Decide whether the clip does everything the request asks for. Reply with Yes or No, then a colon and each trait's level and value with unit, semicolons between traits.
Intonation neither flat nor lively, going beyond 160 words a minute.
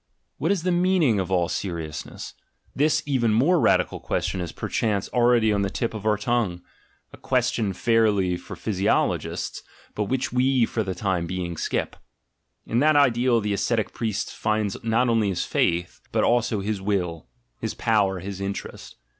Yes: average, 4.1 semitones; average, 170 wpm